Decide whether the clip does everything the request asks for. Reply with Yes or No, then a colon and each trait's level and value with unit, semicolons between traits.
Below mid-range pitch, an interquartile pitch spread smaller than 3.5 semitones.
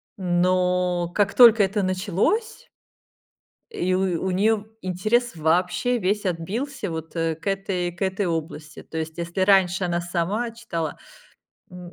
No: medium, 185 Hz; average, 2.9 semitones